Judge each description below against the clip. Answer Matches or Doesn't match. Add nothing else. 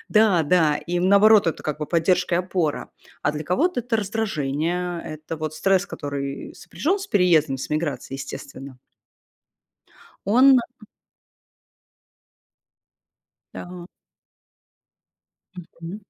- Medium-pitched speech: Matches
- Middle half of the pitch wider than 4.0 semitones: Matches